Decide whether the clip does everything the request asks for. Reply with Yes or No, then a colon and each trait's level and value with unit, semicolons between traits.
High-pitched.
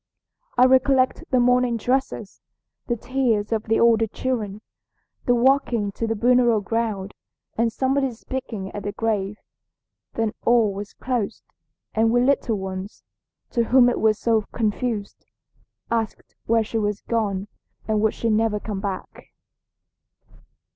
Yes: high, 225 Hz